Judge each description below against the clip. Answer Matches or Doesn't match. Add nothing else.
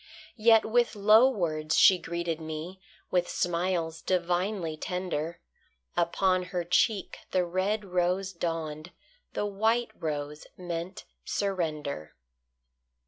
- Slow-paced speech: Matches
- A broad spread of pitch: Doesn't match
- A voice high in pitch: Doesn't match